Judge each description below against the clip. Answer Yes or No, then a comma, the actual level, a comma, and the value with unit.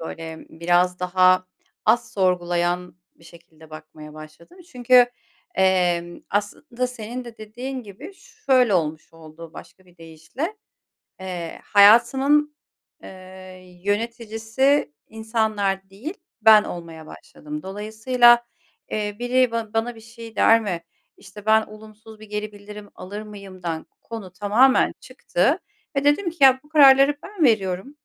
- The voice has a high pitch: Yes, high, 210 Hz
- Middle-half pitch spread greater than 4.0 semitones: Yes, average, 4.9 semitones